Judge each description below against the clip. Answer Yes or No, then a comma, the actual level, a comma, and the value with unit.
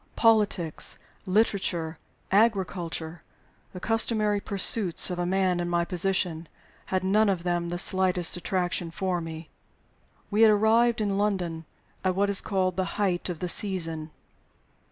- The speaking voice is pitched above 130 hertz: Yes, medium, 185 Hz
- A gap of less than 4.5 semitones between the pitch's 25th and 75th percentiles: Yes, average, 2.8 semitones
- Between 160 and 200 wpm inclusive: No, average, 140 wpm